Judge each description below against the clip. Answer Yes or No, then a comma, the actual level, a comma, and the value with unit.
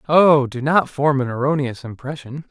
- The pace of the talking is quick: No, average, 170 wpm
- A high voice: No, medium, 140 Hz